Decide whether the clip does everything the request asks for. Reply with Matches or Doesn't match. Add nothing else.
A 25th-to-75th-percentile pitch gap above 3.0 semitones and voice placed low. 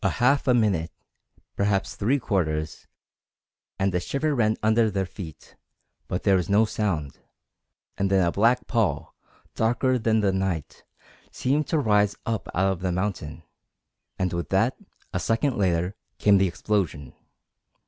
Matches